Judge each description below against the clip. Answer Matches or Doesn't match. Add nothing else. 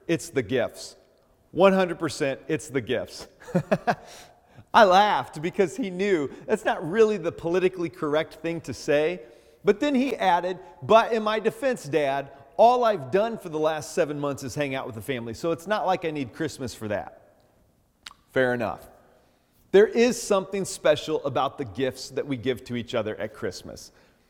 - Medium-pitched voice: Matches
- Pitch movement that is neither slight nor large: Doesn't match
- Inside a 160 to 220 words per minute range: Matches